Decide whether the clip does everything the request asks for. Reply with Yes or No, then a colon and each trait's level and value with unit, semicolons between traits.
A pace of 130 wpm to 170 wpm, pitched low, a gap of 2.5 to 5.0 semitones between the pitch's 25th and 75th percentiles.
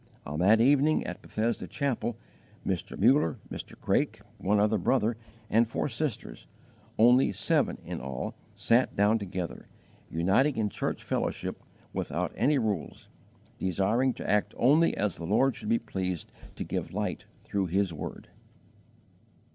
Yes: average, 140 wpm; low, 105 Hz; average, 4.6 semitones